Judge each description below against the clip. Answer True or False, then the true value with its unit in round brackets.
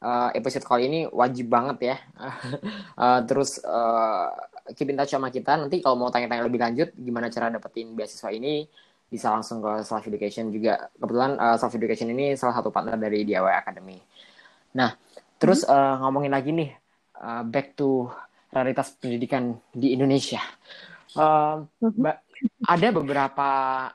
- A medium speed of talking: False (145 wpm)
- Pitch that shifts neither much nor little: True (3.3 semitones)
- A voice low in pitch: True (130 Hz)